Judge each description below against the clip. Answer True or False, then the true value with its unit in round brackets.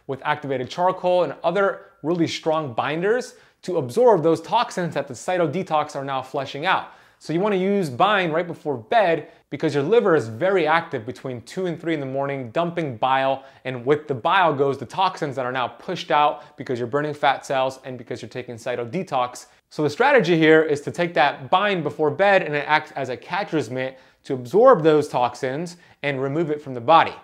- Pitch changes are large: False (4.4 semitones)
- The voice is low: False (150 Hz)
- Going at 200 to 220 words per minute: True (205 wpm)